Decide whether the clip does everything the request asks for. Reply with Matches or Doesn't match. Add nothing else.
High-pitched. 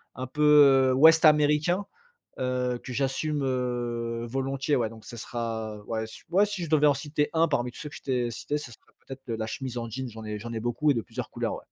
Doesn't match